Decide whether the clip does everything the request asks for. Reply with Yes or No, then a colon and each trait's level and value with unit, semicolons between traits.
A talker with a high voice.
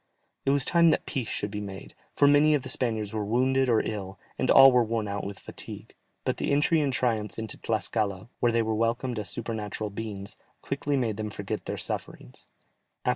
No: low, 115 Hz